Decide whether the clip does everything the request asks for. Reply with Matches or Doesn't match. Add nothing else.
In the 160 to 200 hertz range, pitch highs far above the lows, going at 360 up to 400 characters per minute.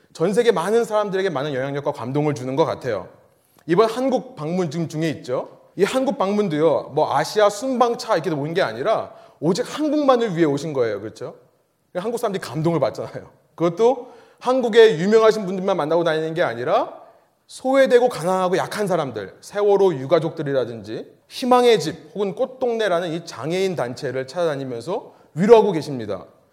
Matches